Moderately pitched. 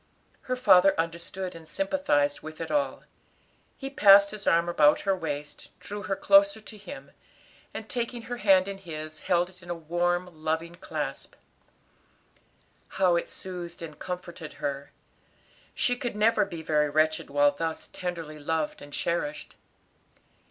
Yes: medium, 175 Hz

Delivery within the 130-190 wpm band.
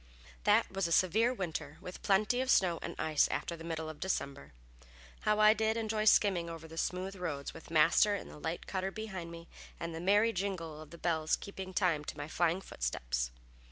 No: average, 200 wpm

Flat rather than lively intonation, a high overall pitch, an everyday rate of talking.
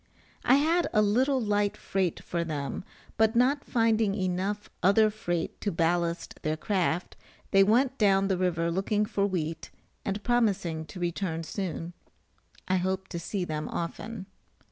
No: average, 3.9 semitones; high, 195 Hz; average, 150 wpm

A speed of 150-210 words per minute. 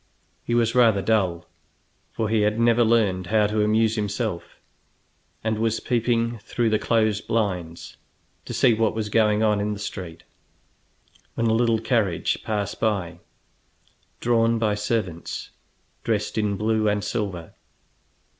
No: average, 140 wpm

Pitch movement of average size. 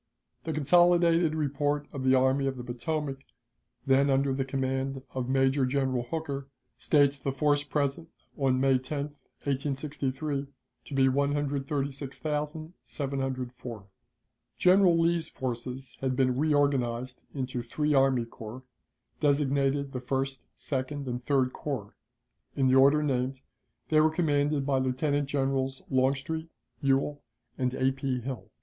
No: narrow, 1.9 semitones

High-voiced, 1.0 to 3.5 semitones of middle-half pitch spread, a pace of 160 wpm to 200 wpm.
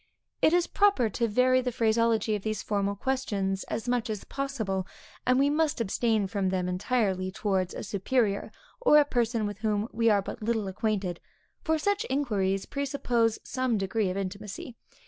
No: high, 220 Hz; average, 4.3 semitones; average, 170 wpm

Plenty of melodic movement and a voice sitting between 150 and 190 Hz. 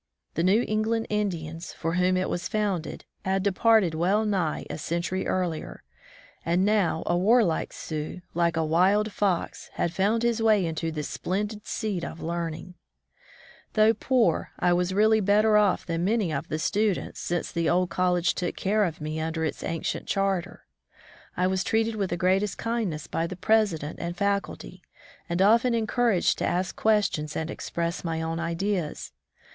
No: average, 3.9 semitones; medium, 185 Hz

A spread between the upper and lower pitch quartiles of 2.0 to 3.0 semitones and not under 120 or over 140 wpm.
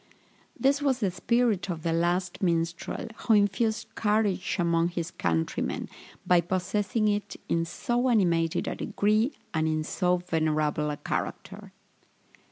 No: average, 4.4 semitones; slow, 135 wpm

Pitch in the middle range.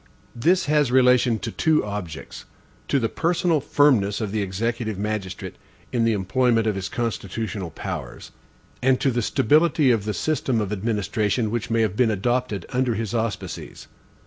No: low, 115 Hz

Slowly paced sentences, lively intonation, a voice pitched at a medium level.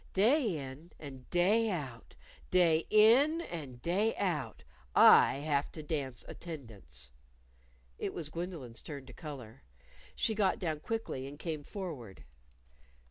Yes: slow, 130 wpm; wide, 6.1 semitones; medium, 155 Hz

